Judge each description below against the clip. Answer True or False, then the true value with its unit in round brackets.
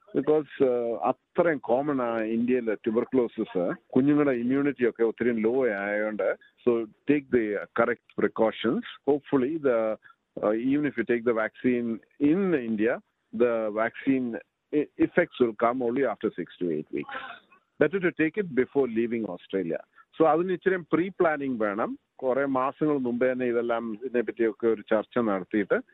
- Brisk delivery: True (135 wpm)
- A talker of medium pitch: False (125 Hz)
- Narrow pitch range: False (3.9 semitones)